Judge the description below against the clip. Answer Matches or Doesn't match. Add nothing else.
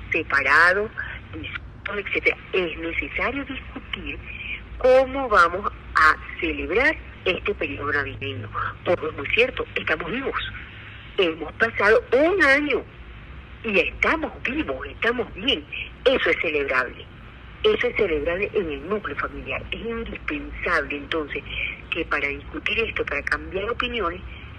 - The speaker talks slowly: Matches